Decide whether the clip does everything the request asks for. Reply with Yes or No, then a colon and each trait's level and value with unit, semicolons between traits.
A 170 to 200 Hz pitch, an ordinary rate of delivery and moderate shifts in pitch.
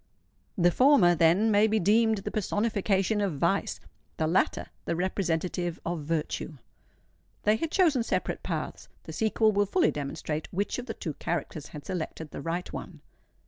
Yes: high, 190 Hz; average, 155 wpm; average, 4.7 semitones